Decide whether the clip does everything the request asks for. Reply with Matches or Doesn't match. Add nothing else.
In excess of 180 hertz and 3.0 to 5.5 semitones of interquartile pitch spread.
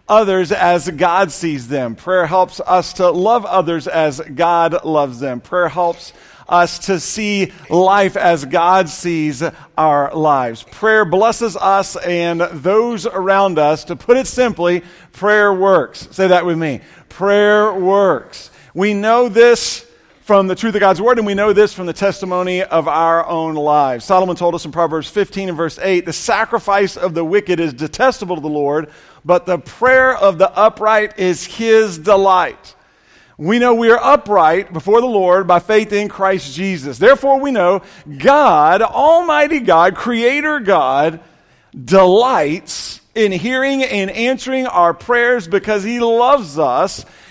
Matches